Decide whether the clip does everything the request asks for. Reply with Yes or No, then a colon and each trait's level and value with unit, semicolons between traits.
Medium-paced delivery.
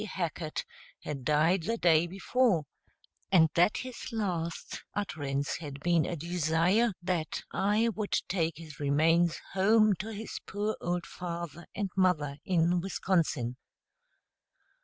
No: slow, 125 wpm